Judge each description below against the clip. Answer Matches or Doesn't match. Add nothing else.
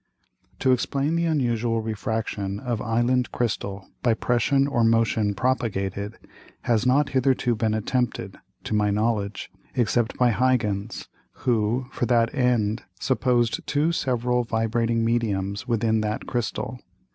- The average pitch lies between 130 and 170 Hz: Doesn't match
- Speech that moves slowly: Matches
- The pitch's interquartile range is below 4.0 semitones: Matches